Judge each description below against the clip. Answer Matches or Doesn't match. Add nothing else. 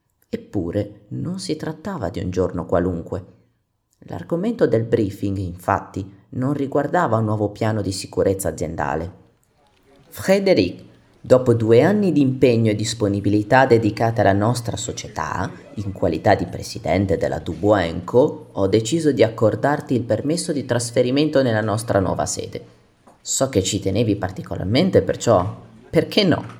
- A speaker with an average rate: Matches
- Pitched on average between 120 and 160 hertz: Doesn't match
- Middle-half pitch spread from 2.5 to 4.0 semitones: Doesn't match